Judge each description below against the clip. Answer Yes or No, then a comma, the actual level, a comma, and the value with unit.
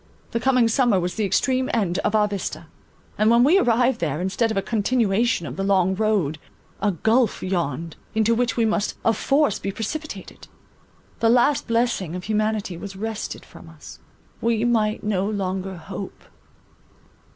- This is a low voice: No, high, 215 Hz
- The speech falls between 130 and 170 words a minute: Yes, average, 165 wpm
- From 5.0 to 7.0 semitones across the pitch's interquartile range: No, average, 3.5 semitones